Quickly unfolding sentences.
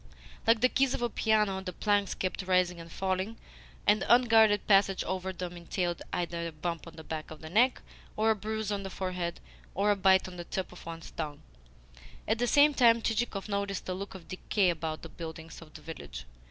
Yes: fast, 210 wpm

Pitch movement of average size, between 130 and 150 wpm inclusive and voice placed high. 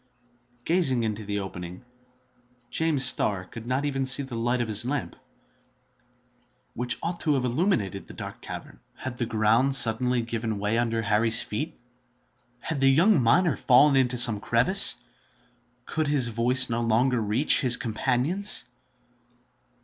No: average, 3.3 semitones; average, 145 wpm; low, 125 Hz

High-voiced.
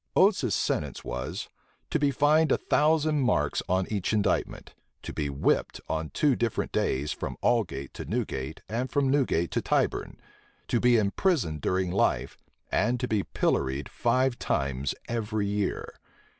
No: low, 110 Hz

